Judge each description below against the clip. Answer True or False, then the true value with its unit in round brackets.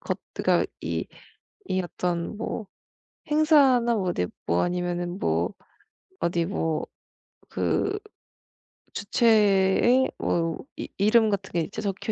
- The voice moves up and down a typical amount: True (4.7 semitones)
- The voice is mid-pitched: False (195 Hz)